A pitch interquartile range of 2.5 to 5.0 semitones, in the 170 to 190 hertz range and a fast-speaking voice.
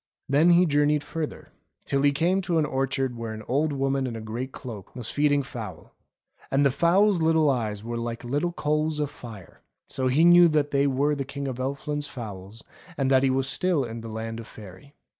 No: average, 4.0 semitones; low, 135 Hz; fast, 210 wpm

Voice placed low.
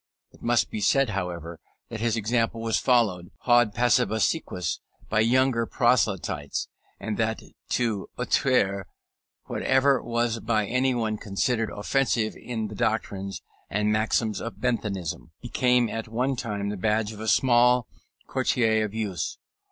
Yes: low, 110 Hz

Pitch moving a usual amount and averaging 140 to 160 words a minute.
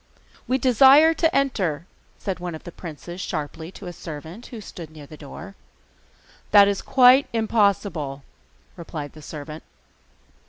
No: wide, 6.4 semitones; average, 145 wpm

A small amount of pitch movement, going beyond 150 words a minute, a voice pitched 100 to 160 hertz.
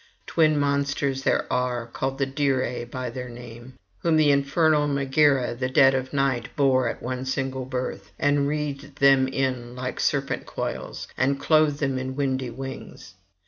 Yes: narrow, 1.8 semitones; average, 160 wpm; low, 135 Hz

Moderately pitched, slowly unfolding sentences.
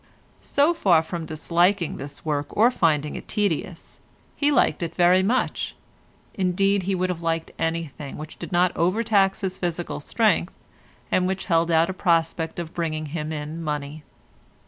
No: medium, 170 Hz; average, 160 wpm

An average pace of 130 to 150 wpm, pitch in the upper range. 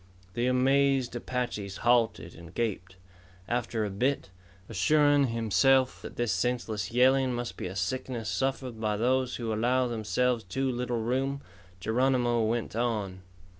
No: slow, 135 wpm; low, 120 Hz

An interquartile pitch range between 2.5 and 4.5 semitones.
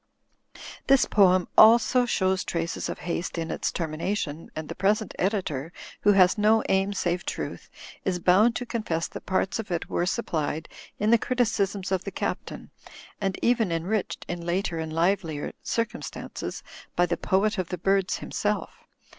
Yes: average, 3.6 semitones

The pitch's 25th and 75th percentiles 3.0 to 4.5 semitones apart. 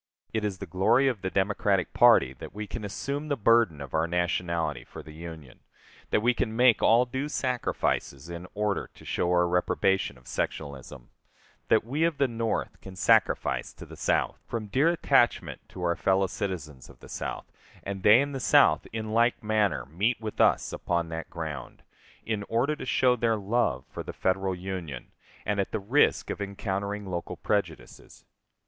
No: average, 5.1 semitones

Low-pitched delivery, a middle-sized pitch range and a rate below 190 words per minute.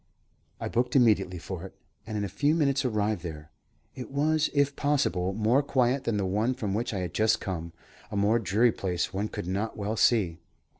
No: low, 110 Hz; average, 4.8 semitones; average, 200 wpm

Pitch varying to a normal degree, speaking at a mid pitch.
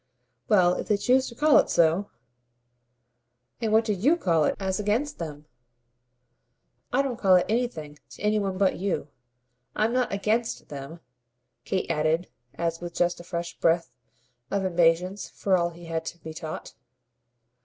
Yes: average, 4.4 semitones; medium, 180 Hz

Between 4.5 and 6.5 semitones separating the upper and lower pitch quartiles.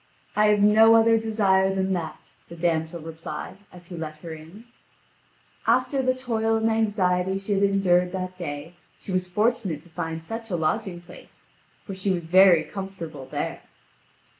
No: average, 4.0 semitones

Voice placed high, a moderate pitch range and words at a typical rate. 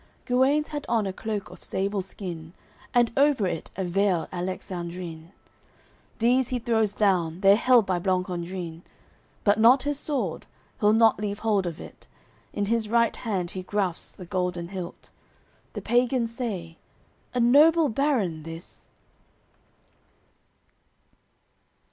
No: high, 205 Hz; average, 4.8 semitones; slow, 130 wpm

